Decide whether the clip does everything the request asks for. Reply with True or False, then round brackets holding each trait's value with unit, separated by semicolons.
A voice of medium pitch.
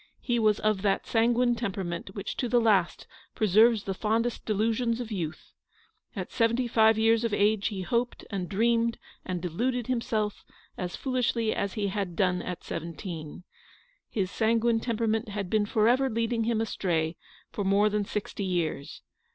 False (215 Hz)